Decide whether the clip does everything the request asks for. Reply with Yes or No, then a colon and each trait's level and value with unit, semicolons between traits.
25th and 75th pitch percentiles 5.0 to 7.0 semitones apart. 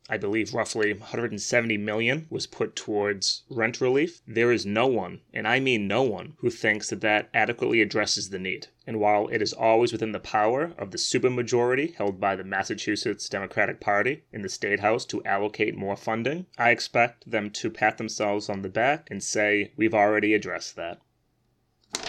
No: narrow, 2.4 semitones